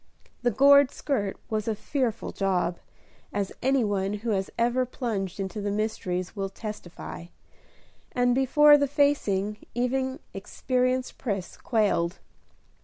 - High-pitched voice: Yes, high, 220 Hz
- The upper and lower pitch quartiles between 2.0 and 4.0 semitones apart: No, average, 4.7 semitones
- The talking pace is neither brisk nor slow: No, slow, 125 wpm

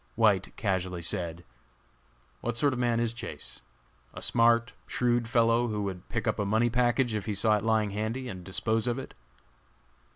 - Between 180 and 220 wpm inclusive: Yes, average, 185 wpm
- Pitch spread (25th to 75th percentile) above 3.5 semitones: No, average, 2.7 semitones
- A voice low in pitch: Yes, low, 115 Hz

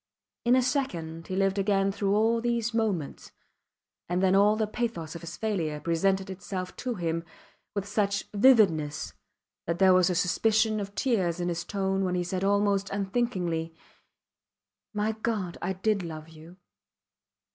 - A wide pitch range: No, average, 3.6 semitones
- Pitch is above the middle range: Yes, high, 195 Hz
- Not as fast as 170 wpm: Yes, average, 155 wpm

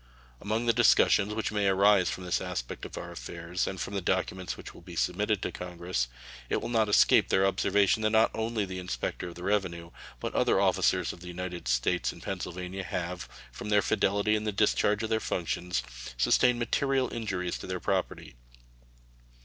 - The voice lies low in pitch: Yes, very low, 95 Hz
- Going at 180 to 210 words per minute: Yes, average, 190 wpm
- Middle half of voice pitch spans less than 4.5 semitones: Yes, average, 3.1 semitones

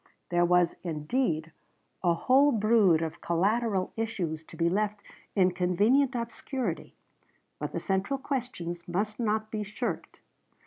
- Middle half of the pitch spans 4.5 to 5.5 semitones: Yes, average, 5.1 semitones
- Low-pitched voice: No, high, 200 Hz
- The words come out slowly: Yes, slow, 130 wpm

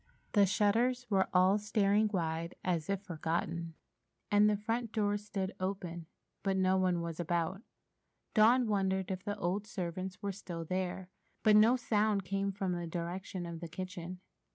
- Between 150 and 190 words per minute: Yes, average, 160 wpm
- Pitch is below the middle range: No, high, 190 Hz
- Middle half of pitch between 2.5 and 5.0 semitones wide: Yes, average, 2.9 semitones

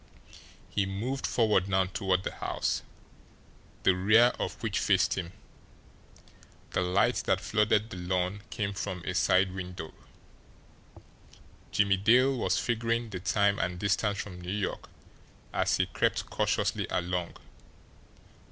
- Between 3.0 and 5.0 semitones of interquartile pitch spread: No, narrow, 2.6 semitones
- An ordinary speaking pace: No, slow, 130 wpm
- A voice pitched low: Yes, very low, 95 Hz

